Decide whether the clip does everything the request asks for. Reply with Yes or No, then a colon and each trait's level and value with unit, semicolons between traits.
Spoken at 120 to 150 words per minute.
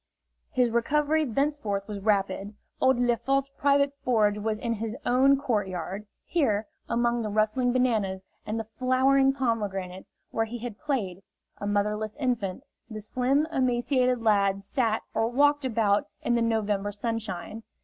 Yes: average, 145 wpm